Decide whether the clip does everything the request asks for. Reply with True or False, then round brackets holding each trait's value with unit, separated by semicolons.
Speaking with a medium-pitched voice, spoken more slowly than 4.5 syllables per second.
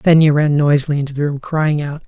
False (150 Hz; 6.0 syllables/s)